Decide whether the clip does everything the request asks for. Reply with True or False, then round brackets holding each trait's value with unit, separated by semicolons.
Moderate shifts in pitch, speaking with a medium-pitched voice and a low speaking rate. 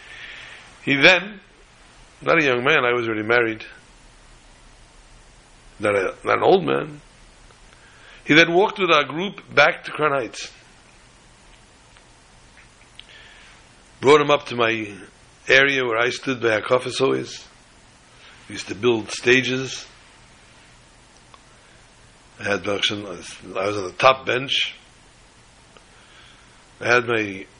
False (4.1 semitones; 120 Hz; 115 wpm)